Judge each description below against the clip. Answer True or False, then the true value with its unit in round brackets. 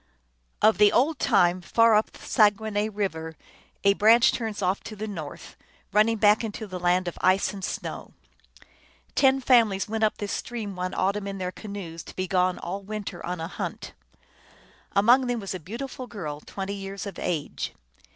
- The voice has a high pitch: True (200 Hz)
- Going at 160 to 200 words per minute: True (180 wpm)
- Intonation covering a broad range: False (2.9 semitones)